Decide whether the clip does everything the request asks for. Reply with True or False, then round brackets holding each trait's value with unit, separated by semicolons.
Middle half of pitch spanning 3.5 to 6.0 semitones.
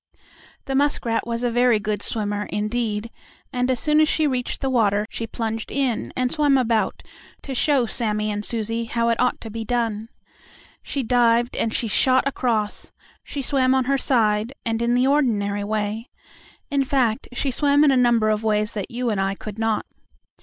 False (3.1 semitones)